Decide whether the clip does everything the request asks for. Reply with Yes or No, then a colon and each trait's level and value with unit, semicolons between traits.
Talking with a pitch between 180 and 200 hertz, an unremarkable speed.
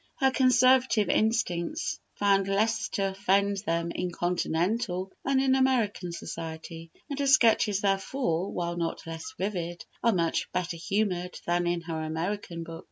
Yes: high, 190 Hz; average, 145 wpm